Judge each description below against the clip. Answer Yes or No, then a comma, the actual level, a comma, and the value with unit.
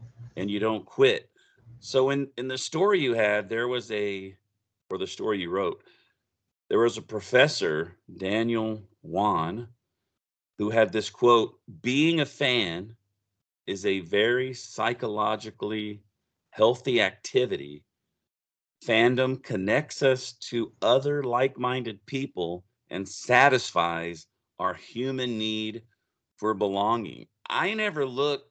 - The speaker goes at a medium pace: No, slow, 115 wpm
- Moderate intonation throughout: Yes, average, 3.7 semitones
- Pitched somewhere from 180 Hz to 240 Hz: No, low, 115 Hz